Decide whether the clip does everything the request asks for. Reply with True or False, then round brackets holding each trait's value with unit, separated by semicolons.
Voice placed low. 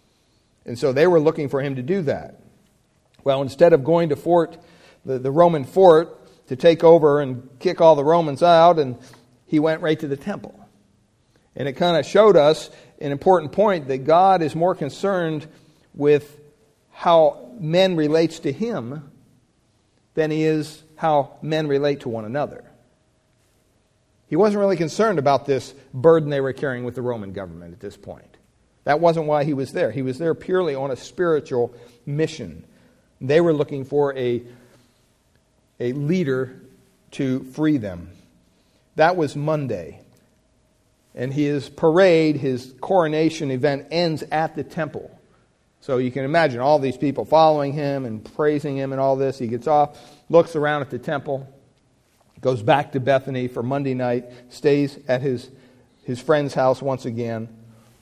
False (145 Hz)